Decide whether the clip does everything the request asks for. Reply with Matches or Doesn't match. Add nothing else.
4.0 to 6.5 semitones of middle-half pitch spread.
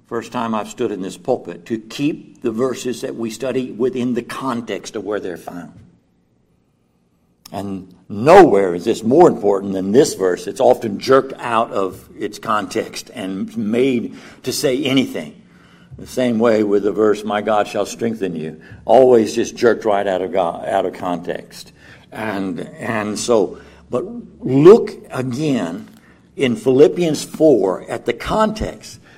Matches